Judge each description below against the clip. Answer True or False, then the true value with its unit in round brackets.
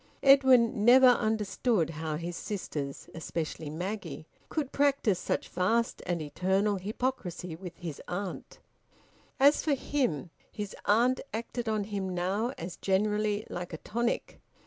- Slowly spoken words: True (130 wpm)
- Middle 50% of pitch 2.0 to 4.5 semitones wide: False (5.1 semitones)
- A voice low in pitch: False (205 Hz)